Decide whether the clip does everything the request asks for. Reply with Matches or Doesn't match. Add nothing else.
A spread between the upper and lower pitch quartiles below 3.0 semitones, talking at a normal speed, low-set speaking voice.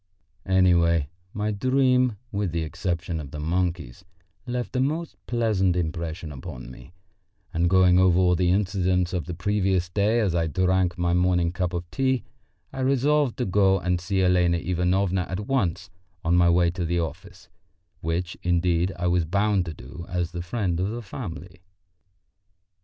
Matches